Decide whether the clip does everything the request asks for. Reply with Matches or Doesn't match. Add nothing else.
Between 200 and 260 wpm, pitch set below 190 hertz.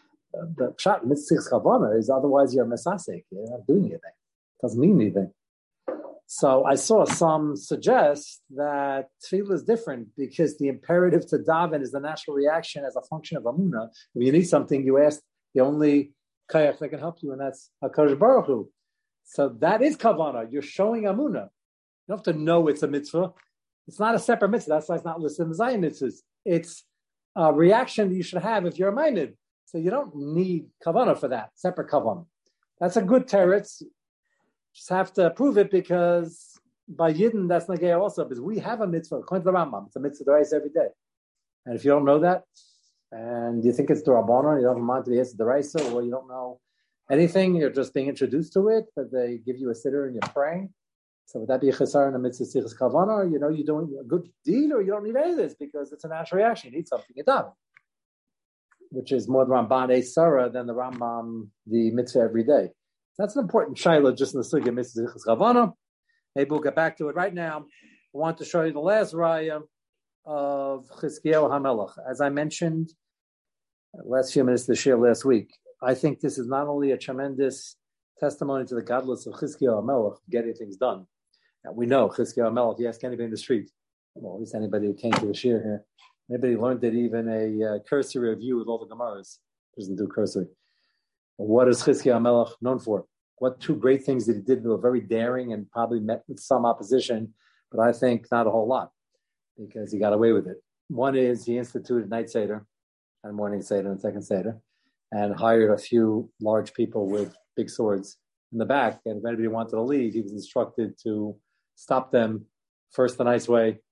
Matches